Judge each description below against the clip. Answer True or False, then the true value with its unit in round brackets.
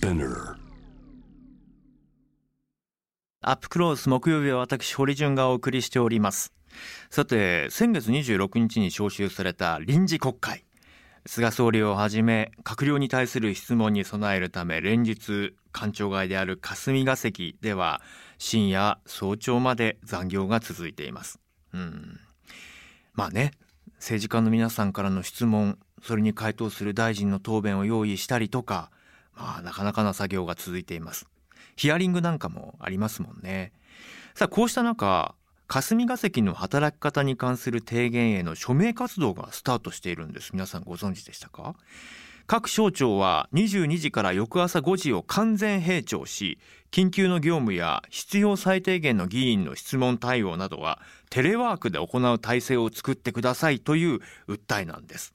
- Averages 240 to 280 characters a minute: False (290 characters per minute)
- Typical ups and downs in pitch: False (6.5 semitones)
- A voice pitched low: True (120 Hz)